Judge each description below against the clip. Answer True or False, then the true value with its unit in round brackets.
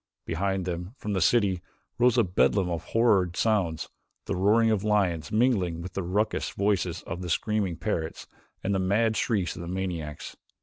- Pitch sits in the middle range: False (95 Hz)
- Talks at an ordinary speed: True (175 wpm)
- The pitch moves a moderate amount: True (3.4 semitones)